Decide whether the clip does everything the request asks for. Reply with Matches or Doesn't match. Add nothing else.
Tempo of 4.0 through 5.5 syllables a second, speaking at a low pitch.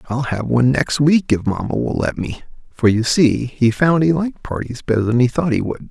Matches